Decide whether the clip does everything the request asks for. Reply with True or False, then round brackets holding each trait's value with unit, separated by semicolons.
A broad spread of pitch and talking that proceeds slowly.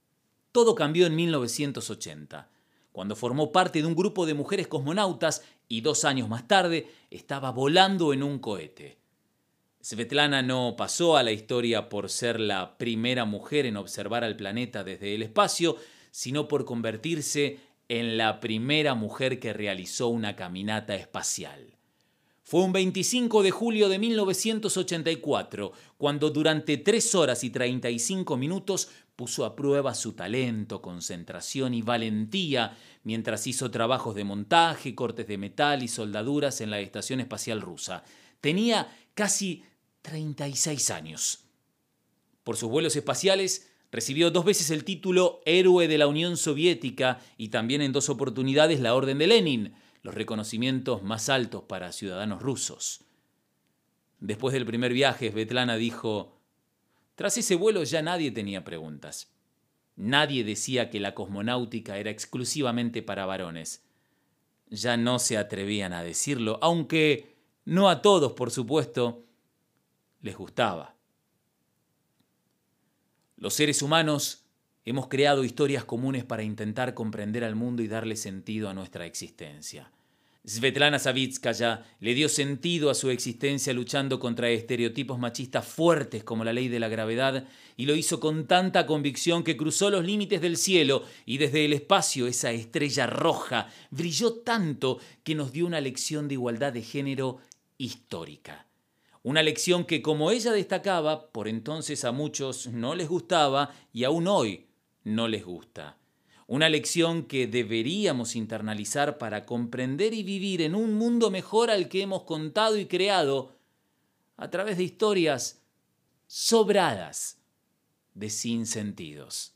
False (5.7 semitones; 140 wpm)